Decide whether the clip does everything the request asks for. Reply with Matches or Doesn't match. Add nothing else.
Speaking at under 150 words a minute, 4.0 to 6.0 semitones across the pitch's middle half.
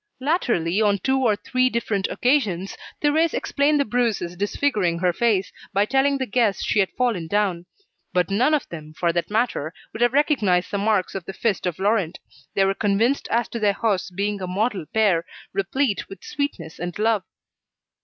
Doesn't match